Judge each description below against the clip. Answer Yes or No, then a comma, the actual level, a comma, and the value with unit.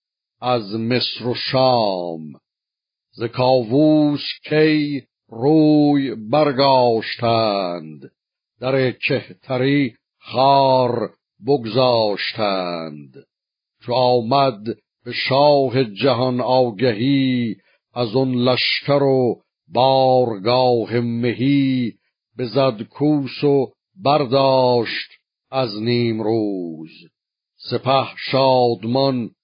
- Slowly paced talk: Yes, slow, 70 wpm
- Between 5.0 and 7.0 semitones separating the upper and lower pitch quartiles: No, average, 2.7 semitones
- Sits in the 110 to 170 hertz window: Yes, low, 125 Hz